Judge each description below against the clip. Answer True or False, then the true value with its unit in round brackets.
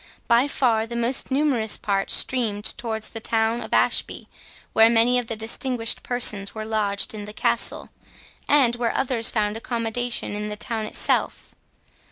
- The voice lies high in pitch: True (225 Hz)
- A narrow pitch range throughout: True (2.0 semitones)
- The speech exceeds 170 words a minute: False (160 wpm)